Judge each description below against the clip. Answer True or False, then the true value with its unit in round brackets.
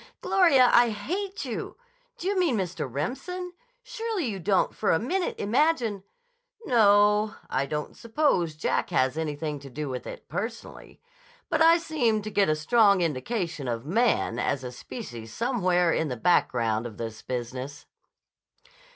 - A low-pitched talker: False (200 Hz)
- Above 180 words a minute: False (150 wpm)